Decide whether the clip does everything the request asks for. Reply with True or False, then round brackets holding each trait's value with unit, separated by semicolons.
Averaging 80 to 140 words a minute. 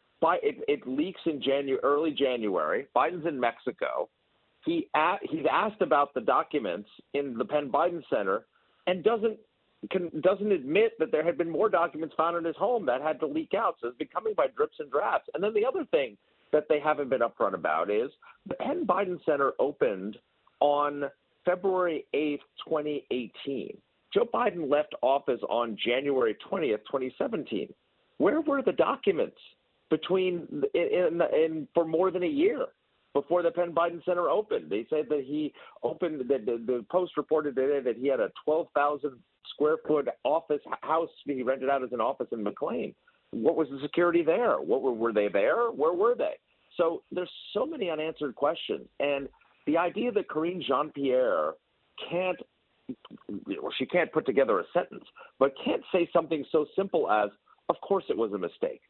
False (180 wpm)